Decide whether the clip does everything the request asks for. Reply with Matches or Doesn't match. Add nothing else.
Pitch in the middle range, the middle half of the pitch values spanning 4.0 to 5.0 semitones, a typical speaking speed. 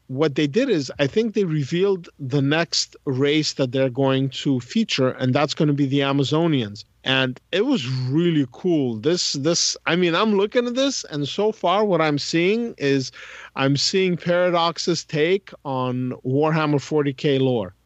Matches